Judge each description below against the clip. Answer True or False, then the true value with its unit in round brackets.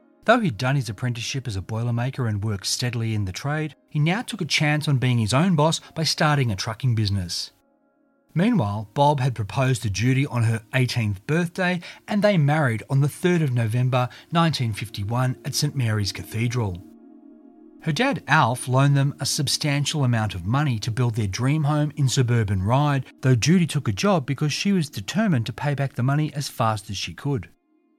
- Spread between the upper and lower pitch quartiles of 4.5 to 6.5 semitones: True (5.1 semitones)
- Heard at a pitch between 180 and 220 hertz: False (135 Hz)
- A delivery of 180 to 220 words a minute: True (190 wpm)